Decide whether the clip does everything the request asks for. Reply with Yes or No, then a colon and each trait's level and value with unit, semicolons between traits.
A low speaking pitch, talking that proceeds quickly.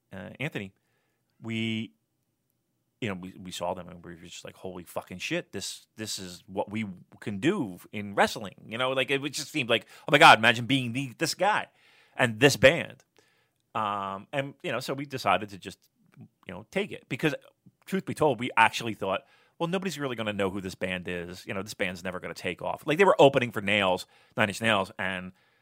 Yes: low, 110 Hz; fast, 220 wpm